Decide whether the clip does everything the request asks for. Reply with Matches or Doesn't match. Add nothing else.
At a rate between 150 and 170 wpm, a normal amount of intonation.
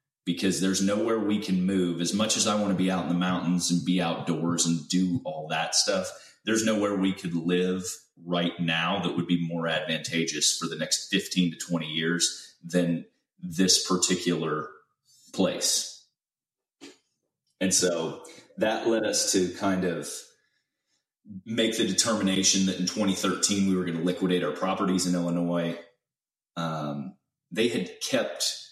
Doesn't match